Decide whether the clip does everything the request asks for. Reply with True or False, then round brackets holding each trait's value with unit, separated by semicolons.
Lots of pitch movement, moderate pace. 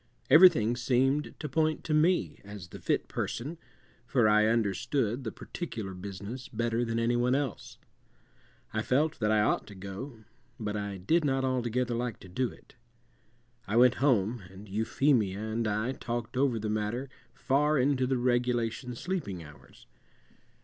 False (3.8 semitones; 155 wpm)